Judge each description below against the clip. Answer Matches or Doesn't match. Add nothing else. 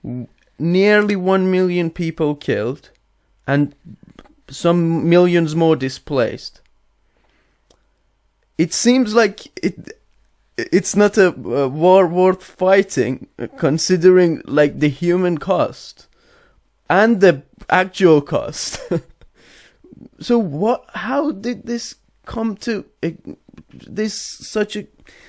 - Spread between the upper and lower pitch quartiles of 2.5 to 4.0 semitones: Doesn't match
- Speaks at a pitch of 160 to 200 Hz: Matches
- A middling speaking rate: Doesn't match